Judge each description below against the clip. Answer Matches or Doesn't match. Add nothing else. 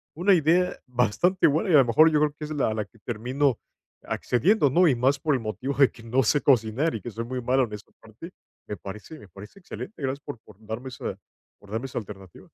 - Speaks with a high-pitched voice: Doesn't match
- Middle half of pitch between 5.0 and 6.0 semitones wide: Matches